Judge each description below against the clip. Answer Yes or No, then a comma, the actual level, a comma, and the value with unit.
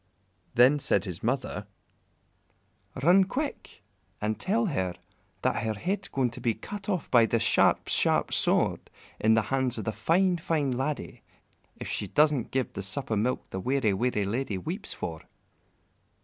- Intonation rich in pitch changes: Yes, wide, 6.3 semitones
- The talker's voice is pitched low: Yes, low, 125 Hz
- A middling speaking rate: Yes, average, 165 wpm